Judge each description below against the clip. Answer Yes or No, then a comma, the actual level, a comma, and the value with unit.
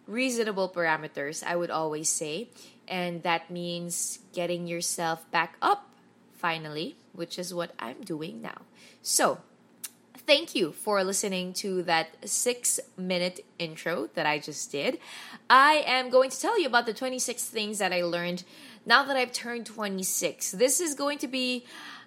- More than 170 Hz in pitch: Yes, high, 190 Hz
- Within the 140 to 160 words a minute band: Yes, average, 155 wpm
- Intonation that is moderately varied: No, wide, 6.5 semitones